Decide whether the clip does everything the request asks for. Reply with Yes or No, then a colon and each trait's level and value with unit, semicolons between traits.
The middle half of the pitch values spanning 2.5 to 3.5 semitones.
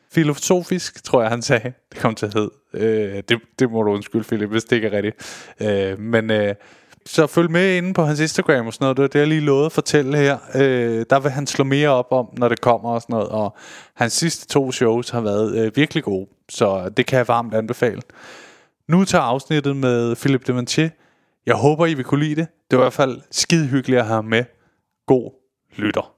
No: average, 4.5 semitones